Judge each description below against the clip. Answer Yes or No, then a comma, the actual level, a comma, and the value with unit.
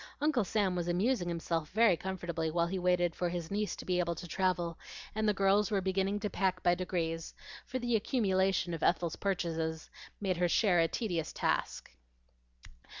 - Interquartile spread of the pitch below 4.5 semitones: Yes, narrow, 2.6 semitones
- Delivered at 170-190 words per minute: Yes, average, 180 wpm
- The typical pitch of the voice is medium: Yes, medium, 180 Hz